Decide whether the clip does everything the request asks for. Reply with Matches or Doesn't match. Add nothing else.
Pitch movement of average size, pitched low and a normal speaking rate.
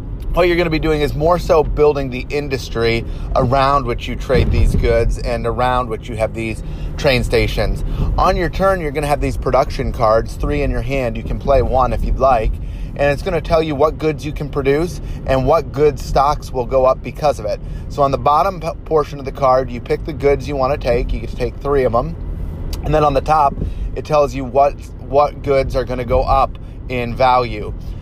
Doesn't match